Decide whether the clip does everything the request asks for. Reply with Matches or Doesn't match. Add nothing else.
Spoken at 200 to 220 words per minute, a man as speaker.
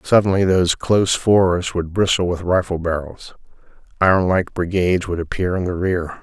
Doesn't match